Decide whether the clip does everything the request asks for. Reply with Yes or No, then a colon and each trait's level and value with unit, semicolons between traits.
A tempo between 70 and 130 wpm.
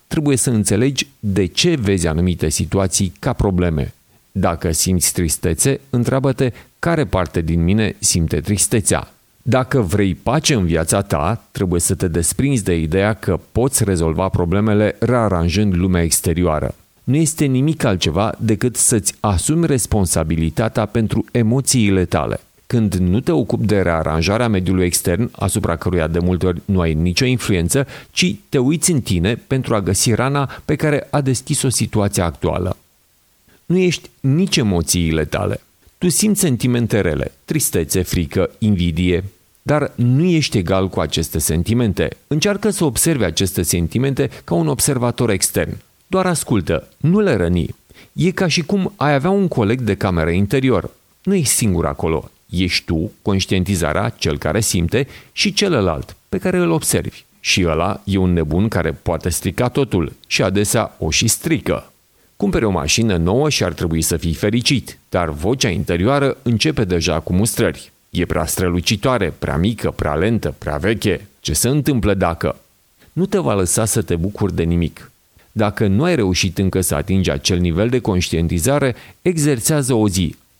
No: fast, 155 wpm